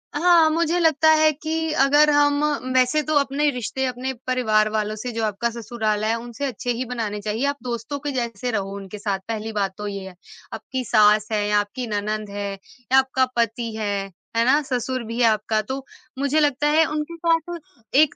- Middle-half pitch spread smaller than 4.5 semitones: No, average, 5.1 semitones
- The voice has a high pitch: Yes, high, 245 Hz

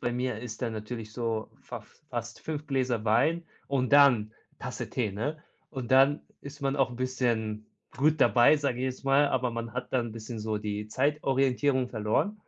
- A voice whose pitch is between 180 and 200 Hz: No, low, 125 Hz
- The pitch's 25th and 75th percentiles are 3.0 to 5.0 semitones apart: Yes, average, 3.5 semitones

